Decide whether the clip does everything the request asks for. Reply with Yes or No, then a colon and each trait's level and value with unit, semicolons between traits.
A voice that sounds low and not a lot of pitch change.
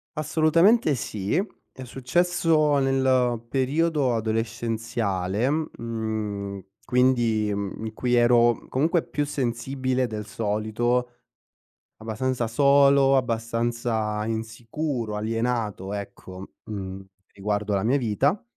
No: low, 120 Hz; average, 3.7 semitones